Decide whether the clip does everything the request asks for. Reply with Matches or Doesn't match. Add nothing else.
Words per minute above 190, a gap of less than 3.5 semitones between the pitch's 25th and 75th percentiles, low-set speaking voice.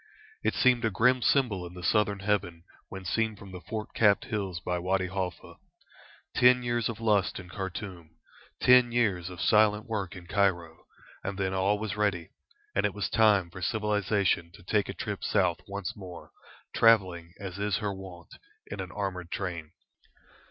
Doesn't match